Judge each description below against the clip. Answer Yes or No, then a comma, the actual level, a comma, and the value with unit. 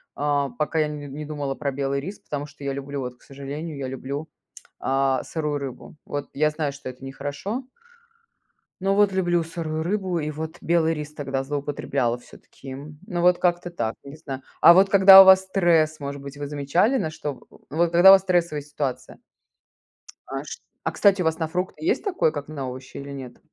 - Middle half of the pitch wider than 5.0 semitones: No, average, 3.7 semitones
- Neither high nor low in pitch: Yes, medium, 150 Hz